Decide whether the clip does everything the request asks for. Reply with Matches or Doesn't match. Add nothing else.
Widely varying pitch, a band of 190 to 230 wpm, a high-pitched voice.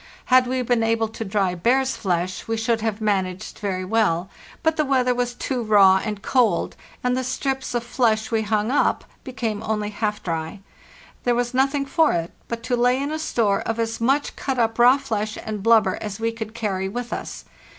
Doesn't match